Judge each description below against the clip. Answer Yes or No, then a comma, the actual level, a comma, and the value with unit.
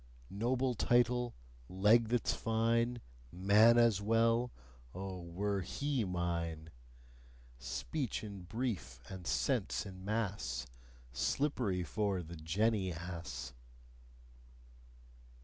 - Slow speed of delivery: Yes, slow, 95 wpm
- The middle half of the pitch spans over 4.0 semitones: Yes, average, 5.0 semitones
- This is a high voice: No, low, 100 Hz